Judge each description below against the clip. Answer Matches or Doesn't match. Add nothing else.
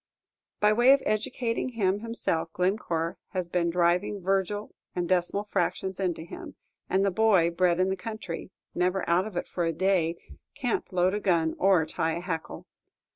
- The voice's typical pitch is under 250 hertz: Matches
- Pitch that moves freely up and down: Doesn't match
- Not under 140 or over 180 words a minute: Matches